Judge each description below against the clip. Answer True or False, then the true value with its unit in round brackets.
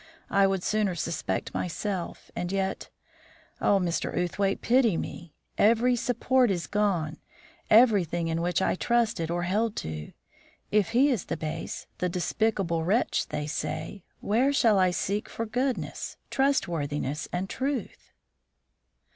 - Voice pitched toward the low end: False (195 Hz)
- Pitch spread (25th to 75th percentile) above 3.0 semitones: True (5.0 semitones)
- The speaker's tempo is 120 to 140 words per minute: True (135 wpm)